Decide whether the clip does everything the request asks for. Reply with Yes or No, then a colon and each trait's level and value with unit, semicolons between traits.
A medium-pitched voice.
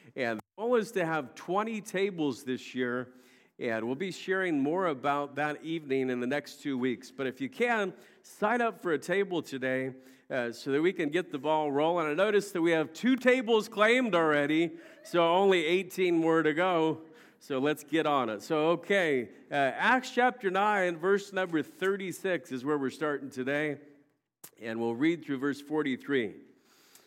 Yes: medium, 160 Hz